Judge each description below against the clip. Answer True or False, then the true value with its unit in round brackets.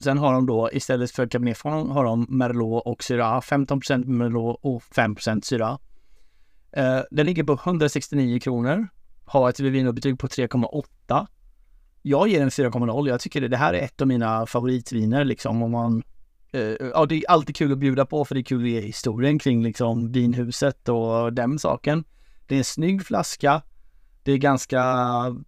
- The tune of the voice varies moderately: True (3.0 semitones)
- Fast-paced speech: False (175 wpm)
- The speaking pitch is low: True (130 Hz)